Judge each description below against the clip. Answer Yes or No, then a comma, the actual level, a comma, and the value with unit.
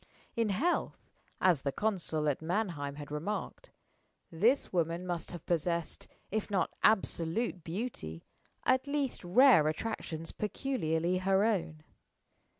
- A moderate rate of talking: No, slow, 120 wpm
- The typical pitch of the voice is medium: Yes, medium, 180 Hz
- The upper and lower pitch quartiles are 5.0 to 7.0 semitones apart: Yes, average, 5.3 semitones